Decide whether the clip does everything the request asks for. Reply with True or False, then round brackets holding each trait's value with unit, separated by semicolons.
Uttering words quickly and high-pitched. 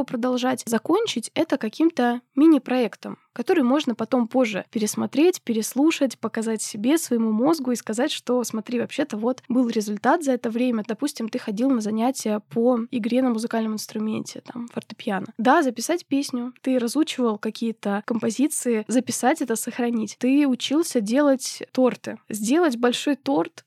False (140 wpm; 245 Hz)